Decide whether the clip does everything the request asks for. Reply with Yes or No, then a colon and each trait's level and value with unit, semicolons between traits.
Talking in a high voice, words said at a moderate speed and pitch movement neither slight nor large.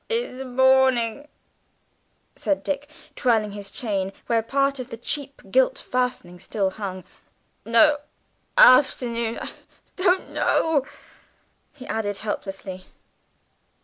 No: very high, 250 Hz; slow, 110 wpm; average, 4.8 semitones